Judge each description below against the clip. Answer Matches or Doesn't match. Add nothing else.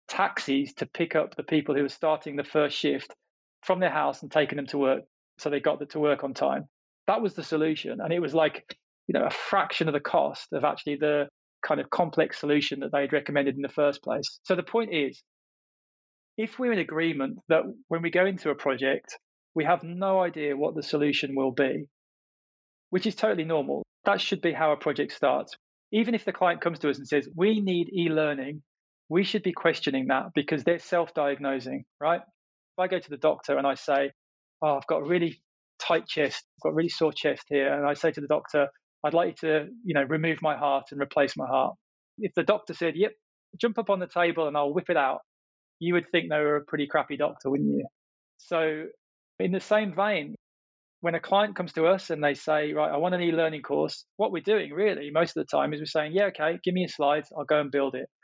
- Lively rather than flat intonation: Doesn't match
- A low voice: Doesn't match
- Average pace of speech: Doesn't match